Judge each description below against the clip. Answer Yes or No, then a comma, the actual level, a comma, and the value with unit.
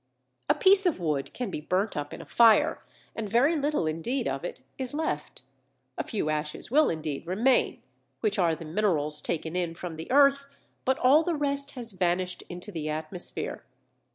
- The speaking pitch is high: Yes, high, 195 Hz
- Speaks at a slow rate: No, average, 180 wpm